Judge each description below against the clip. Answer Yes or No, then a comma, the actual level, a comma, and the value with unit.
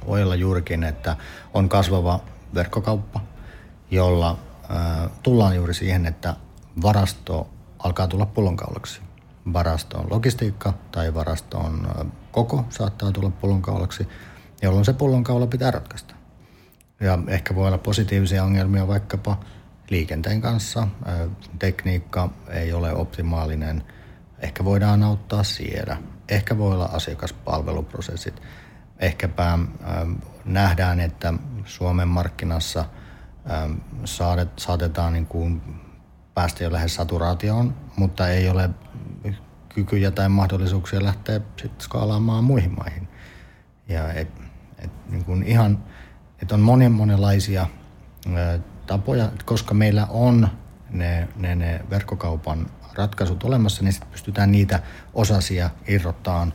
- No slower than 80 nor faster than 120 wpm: Yes, average, 110 wpm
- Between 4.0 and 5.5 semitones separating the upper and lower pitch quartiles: No, average, 3.2 semitones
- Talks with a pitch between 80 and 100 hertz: Yes, very low, 95 Hz